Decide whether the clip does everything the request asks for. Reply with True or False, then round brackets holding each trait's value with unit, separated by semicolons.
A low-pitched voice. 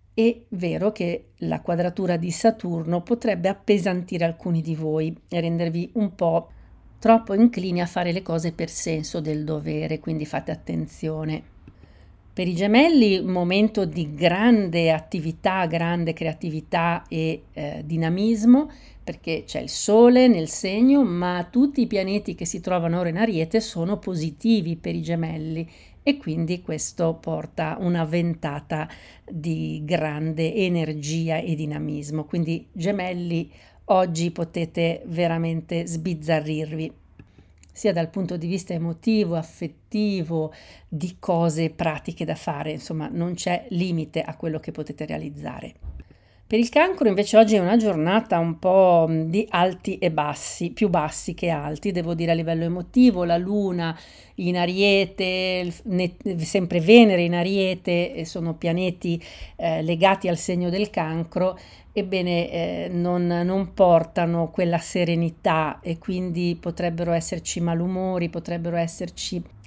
False (175 Hz)